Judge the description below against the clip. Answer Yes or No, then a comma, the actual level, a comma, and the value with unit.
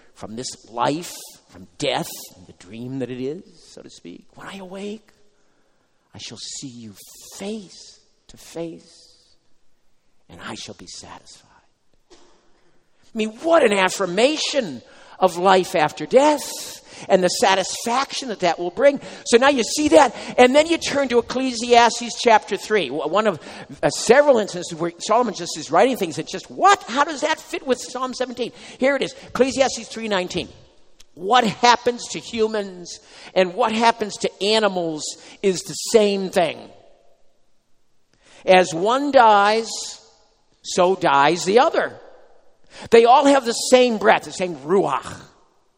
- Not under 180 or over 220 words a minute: No, average, 150 wpm